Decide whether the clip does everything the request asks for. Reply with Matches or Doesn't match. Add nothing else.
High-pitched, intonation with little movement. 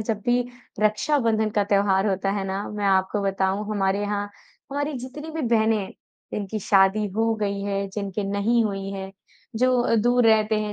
Matches